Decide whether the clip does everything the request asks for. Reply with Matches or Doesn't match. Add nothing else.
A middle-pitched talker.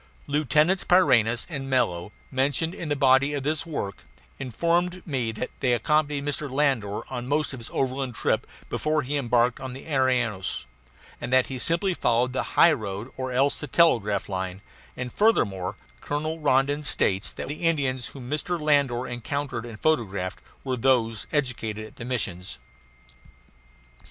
Doesn't match